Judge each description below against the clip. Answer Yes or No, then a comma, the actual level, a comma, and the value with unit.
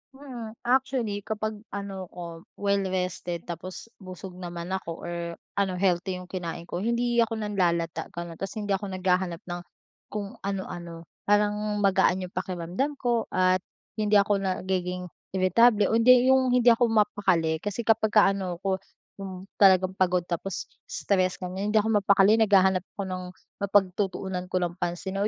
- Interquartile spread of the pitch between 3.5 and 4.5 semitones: No, narrow, 2.5 semitones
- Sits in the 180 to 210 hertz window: Yes, high, 190 Hz